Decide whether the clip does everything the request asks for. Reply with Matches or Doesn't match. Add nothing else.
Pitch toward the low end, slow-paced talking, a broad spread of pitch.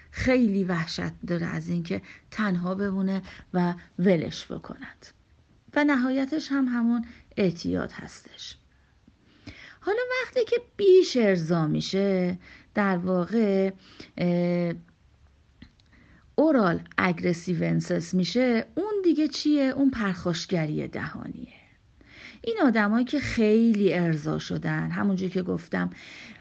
Doesn't match